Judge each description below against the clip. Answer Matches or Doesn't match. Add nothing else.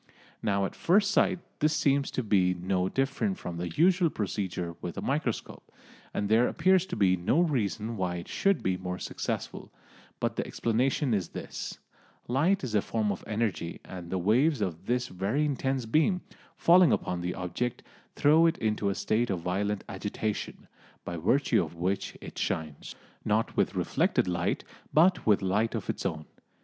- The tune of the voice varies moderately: Doesn't match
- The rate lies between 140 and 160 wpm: Doesn't match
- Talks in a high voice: Doesn't match